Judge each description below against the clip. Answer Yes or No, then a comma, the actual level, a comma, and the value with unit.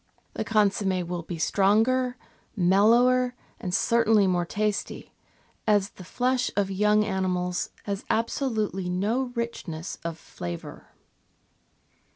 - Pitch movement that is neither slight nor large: Yes, average, 4.0 semitones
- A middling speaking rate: No, slow, 110 wpm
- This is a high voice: Yes, high, 205 Hz